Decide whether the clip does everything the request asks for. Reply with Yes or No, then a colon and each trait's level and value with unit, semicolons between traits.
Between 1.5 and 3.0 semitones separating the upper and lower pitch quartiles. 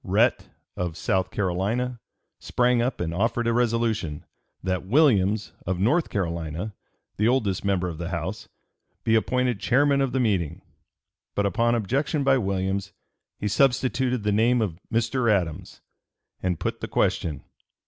No: average, 4.8 semitones